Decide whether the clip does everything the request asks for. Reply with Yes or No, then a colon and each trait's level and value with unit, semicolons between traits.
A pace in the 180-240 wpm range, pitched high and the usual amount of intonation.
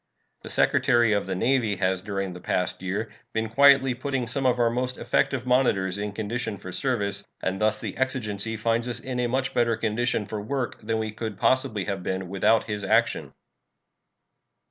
No: average, 185 wpm; low, 110 Hz; average, 3.5 semitones